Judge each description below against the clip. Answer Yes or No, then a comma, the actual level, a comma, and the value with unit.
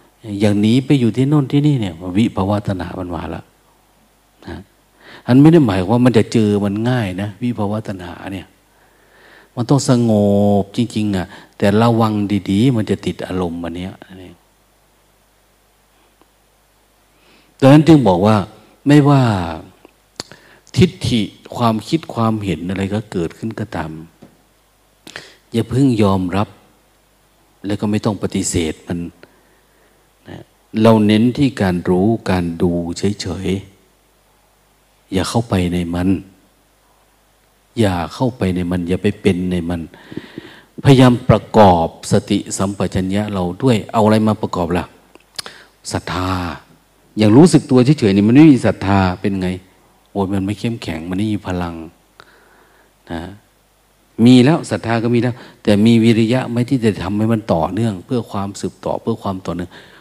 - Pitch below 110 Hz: Yes, low, 100 Hz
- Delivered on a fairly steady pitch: No, average, 4.0 semitones